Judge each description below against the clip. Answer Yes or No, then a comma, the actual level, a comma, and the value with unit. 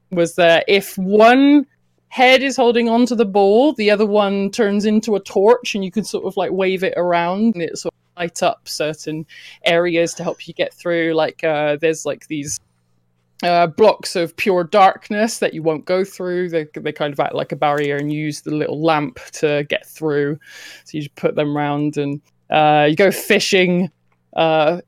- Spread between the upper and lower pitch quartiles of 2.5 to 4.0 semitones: No, average, 4.8 semitones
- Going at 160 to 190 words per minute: No, average, 200 wpm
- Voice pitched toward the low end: No, medium, 170 Hz